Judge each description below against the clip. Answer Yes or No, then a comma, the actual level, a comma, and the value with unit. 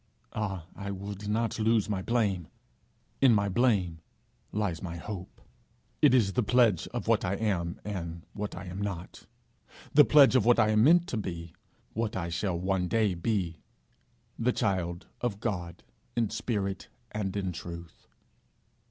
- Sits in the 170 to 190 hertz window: No, low, 100 Hz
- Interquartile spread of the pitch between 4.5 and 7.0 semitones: No, average, 3.9 semitones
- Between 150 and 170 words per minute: Yes, average, 160 wpm